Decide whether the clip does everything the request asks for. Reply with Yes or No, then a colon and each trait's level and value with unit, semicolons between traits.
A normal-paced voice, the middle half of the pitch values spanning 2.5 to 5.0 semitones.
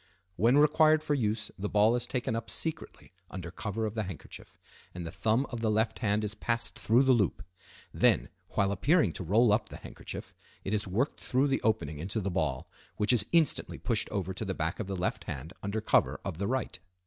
No: fast, 215 wpm; average, 4.0 semitones